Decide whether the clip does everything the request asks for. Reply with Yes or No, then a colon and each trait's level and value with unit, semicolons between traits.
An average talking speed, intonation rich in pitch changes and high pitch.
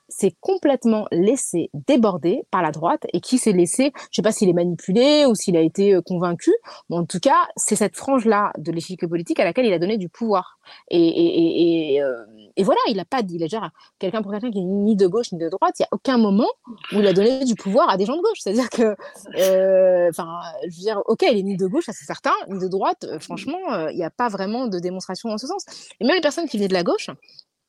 No: fast, 265 wpm; wide, 6.4 semitones; high, 210 Hz